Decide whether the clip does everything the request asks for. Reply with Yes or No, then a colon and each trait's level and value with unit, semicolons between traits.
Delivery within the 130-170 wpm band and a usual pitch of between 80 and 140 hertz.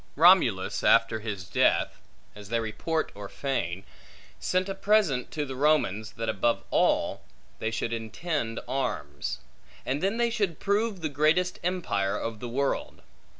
Yes: average, 150 wpm; low, 135 Hz